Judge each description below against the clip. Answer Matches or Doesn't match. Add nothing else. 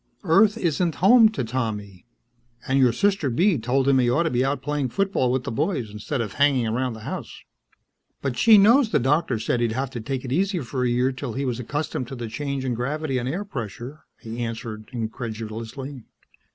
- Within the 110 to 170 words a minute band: Doesn't match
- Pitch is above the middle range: Doesn't match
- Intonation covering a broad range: Doesn't match